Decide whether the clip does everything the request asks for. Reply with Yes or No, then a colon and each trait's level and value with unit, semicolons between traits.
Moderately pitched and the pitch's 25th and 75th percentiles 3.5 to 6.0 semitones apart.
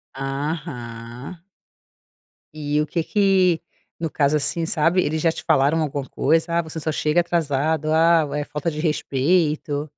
No: medium, 155 Hz; narrow, 2.4 semitones